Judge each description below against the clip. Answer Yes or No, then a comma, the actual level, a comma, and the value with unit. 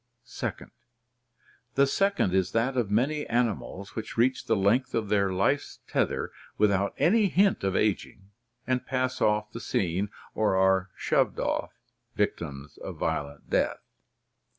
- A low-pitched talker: Yes, low, 105 Hz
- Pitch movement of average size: Yes, average, 5.0 semitones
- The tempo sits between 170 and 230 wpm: No, average, 150 wpm